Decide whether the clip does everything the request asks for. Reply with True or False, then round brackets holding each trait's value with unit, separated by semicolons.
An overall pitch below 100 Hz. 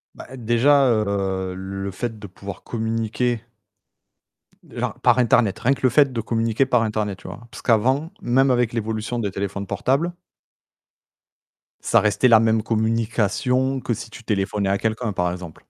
False (115 Hz)